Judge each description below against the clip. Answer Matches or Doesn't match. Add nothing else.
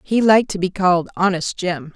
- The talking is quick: Matches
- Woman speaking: Matches